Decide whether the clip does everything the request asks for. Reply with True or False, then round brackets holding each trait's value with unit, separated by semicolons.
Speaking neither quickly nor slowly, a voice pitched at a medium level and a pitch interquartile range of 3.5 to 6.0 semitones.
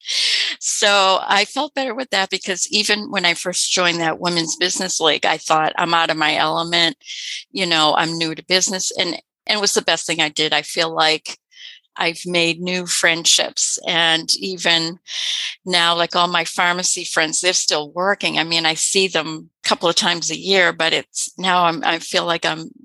False (195 wpm; 175 Hz; 2.5 semitones)